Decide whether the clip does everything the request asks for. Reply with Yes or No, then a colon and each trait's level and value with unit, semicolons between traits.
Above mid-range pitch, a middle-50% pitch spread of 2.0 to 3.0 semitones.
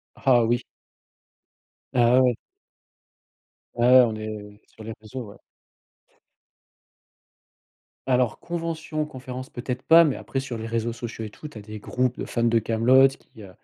No: low, 120 Hz; narrow, 2.6 semitones